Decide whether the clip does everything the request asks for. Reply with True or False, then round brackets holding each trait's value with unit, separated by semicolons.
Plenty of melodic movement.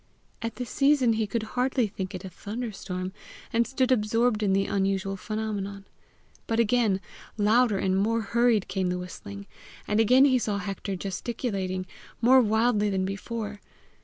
False (3.2 semitones)